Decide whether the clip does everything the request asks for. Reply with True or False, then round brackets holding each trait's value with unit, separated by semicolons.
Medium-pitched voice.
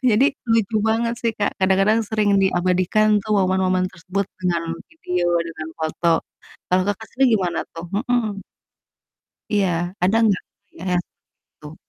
False (195 Hz)